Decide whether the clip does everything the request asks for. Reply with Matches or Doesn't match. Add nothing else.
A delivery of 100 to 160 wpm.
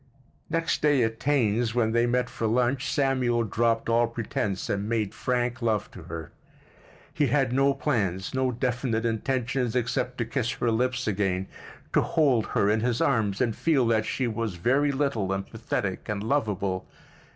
Doesn't match